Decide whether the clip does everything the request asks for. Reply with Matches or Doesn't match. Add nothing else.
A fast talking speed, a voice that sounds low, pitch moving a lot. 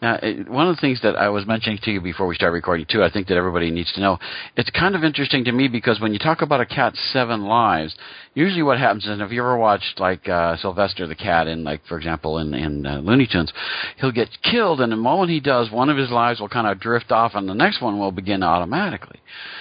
Matches